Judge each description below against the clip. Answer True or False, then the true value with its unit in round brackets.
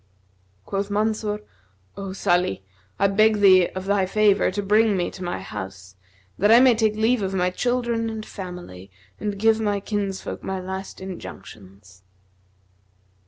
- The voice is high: True (195 Hz)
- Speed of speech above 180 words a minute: False (150 wpm)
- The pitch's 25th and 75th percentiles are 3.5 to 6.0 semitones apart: False (2.9 semitones)